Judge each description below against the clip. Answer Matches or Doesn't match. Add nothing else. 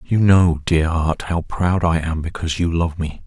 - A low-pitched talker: Matches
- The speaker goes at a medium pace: Doesn't match